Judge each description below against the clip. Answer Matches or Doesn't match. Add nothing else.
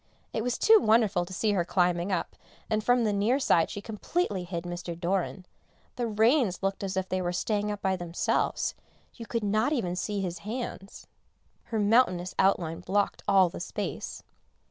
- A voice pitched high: Matches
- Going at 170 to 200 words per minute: Matches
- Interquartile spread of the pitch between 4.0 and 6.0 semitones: Doesn't match